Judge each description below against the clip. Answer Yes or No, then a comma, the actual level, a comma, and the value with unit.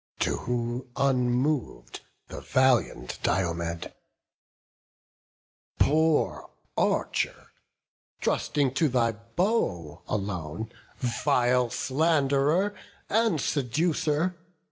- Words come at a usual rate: No, slow, 70 wpm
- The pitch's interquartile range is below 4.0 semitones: No, average, 5.1 semitones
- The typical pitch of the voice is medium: No, low, 130 Hz